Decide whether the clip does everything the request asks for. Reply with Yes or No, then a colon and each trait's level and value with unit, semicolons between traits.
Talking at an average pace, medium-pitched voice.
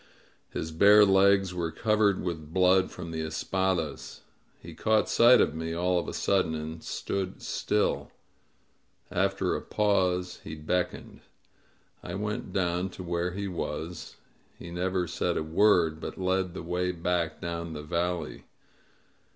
No: average, 145 wpm; very low, 90 Hz